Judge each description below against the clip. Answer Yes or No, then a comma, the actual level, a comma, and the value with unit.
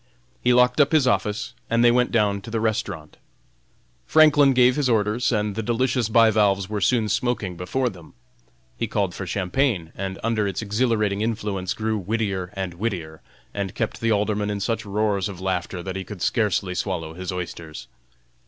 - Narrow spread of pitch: No, average, 3.4 semitones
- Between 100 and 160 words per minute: No, average, 175 wpm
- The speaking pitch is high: No, low, 105 Hz